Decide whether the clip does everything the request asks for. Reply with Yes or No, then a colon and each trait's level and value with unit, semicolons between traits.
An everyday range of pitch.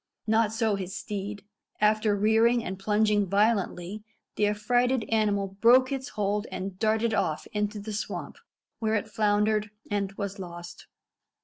No: narrow, 1.6 semitones